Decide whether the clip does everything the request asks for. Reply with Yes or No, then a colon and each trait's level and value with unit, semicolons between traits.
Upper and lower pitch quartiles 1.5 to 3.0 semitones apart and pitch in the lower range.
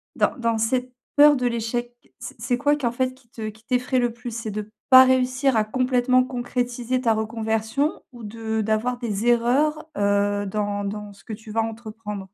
No: narrow, 2.6 semitones; high, 235 Hz